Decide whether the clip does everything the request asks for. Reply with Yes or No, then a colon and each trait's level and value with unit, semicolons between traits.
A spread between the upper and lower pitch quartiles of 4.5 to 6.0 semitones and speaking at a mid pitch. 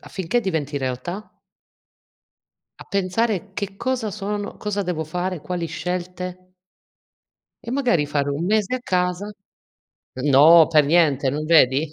Yes: average, 4.8 semitones; medium, 180 Hz